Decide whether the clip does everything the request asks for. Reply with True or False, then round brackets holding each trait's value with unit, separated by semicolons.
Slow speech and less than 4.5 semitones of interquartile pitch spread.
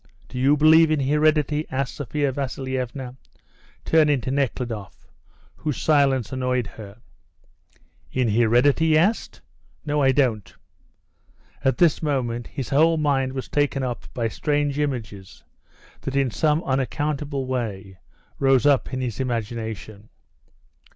True (125 wpm; 3.4 semitones)